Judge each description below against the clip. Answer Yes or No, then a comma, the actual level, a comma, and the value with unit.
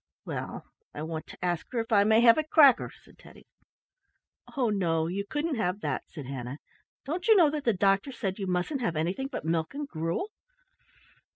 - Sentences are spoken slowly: No, average, 195 wpm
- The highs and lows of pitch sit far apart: Yes, wide, 8.3 semitones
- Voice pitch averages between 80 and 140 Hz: No, high, 200 Hz